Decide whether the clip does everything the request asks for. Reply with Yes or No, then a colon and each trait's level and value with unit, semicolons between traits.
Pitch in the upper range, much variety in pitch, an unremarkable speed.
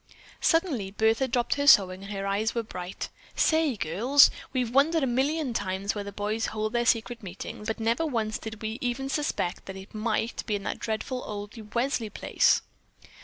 No: high, 225 Hz; average, 3.9 semitones; average, 185 wpm